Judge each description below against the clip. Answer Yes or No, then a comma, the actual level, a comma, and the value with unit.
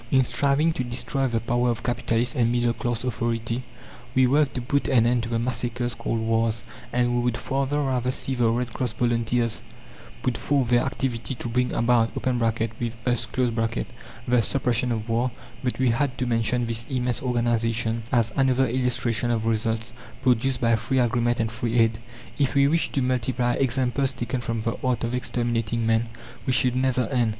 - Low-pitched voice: Yes, low, 120 Hz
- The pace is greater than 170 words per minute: Yes, average, 180 wpm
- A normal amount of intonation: No, narrow, 1.8 semitones